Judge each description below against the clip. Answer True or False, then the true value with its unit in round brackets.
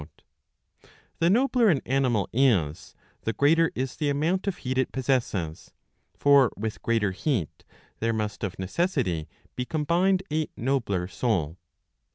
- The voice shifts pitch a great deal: True (7.0 semitones)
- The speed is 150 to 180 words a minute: False (140 wpm)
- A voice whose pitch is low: True (130 Hz)